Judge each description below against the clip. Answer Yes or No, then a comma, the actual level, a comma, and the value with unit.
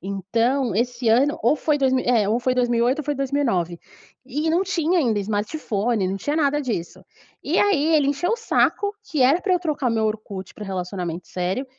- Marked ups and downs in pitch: Yes, wide, 6.2 semitones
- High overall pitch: Yes, very high, 250 Hz